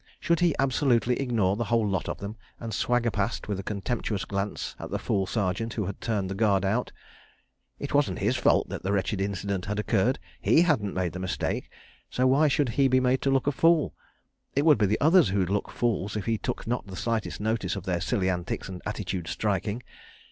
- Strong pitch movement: No, average, 4.3 semitones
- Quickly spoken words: Yes, fast, 220 wpm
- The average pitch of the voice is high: No, low, 110 Hz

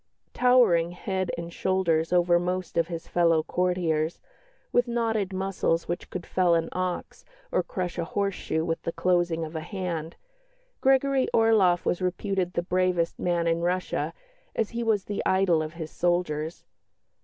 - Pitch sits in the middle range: Yes, medium, 180 Hz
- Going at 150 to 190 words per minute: Yes, average, 160 wpm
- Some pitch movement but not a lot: No, narrow, 2.2 semitones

